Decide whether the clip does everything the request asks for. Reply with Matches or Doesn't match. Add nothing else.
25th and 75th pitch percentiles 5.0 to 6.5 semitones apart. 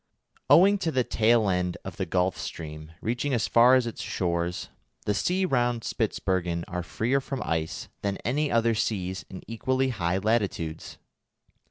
Matches